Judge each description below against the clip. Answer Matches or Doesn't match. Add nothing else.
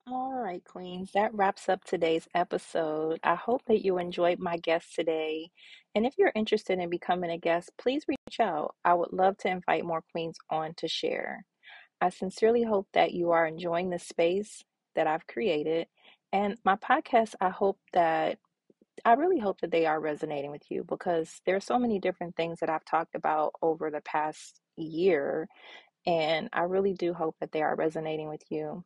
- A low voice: Doesn't match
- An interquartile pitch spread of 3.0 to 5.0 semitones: Matches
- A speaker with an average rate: Matches